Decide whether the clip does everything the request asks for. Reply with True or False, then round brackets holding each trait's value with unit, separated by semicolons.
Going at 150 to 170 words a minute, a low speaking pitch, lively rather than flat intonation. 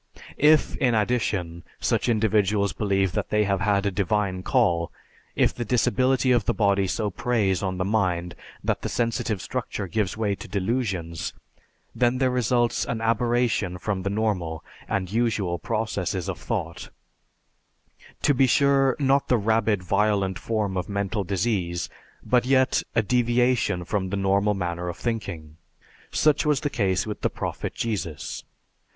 False (155 wpm; 105 Hz; 4.2 semitones)